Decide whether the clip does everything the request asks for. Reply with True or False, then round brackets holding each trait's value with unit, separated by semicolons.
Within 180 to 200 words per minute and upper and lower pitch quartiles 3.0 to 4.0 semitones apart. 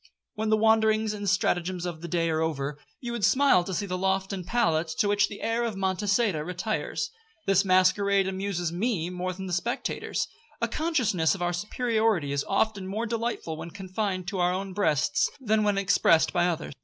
True (190 wpm; 3.6 semitones)